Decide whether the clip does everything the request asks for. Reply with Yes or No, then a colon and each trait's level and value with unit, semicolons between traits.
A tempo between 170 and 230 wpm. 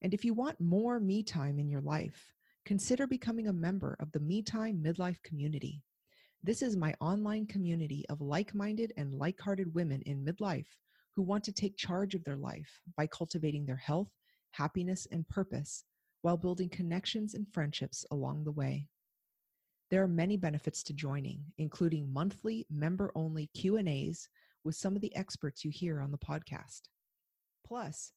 No: average, 160 wpm